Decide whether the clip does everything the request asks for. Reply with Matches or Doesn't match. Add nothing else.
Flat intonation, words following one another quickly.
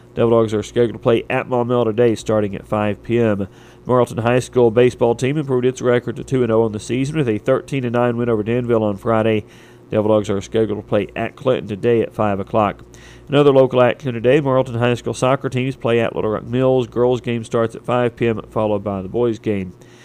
Matches